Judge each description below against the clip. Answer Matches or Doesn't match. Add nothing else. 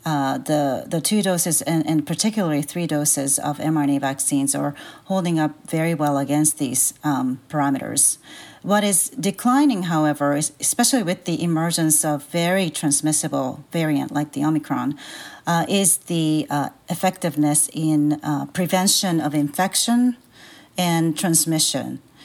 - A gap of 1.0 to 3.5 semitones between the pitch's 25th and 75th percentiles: Matches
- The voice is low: Doesn't match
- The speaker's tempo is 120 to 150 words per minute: Matches